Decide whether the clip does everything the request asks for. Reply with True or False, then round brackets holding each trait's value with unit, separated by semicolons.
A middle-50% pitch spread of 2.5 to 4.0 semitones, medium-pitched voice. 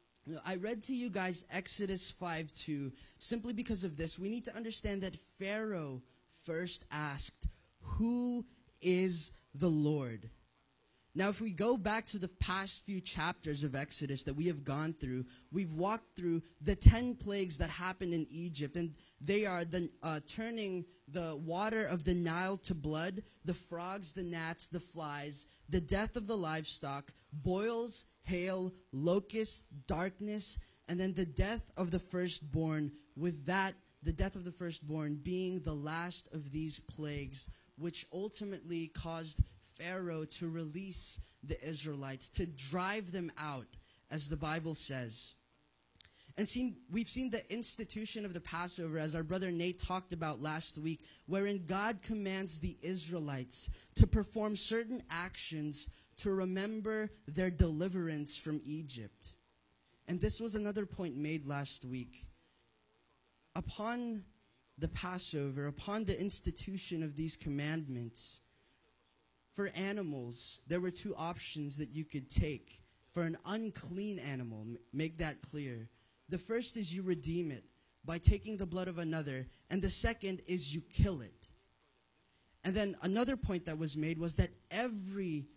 False (4.4 semitones; 170 Hz)